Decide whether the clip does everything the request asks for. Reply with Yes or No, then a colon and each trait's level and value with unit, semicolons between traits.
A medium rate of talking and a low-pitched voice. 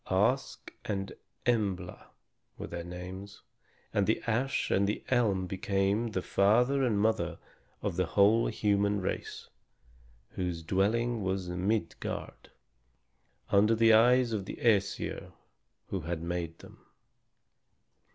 No: slow, 120 wpm; low, 100 Hz